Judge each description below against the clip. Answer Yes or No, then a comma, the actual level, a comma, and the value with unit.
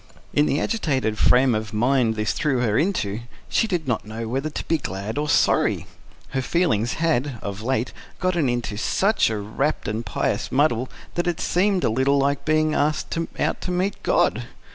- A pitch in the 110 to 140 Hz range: Yes, low, 135 Hz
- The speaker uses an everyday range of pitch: No, wide, 5.8 semitones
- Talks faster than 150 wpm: Yes, average, 185 wpm